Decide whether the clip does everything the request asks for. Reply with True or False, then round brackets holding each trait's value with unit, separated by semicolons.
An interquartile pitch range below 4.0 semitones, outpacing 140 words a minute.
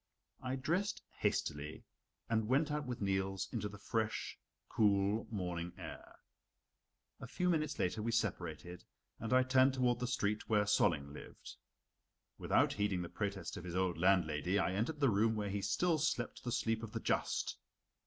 False (4.8 semitones; 165 wpm)